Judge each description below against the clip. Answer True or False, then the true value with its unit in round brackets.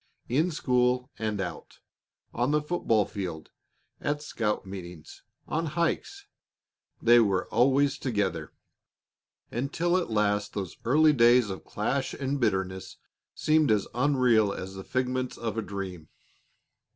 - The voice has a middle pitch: False (120 Hz)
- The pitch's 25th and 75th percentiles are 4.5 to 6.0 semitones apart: True (5.6 semitones)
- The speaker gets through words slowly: True (125 wpm)